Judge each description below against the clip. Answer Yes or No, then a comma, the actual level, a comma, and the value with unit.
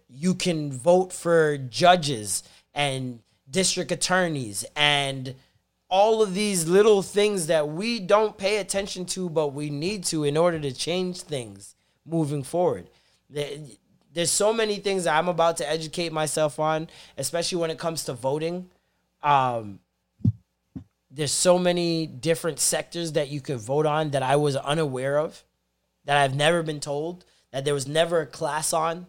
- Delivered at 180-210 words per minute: No, average, 155 wpm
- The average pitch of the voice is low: No, medium, 160 Hz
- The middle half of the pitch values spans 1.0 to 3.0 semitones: No, average, 3.7 semitones